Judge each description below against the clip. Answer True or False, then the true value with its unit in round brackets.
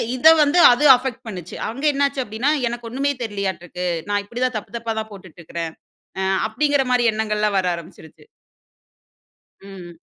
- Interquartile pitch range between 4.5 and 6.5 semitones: True (5.0 semitones)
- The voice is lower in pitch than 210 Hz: False (220 Hz)